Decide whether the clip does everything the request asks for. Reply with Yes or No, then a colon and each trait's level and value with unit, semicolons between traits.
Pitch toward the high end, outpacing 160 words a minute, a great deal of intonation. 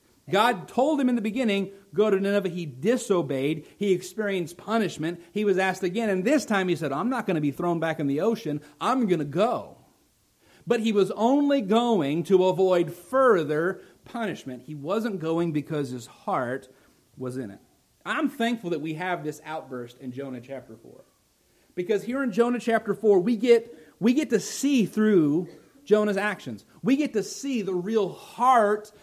Yes: high, 195 Hz; average, 180 wpm; wide, 6.3 semitones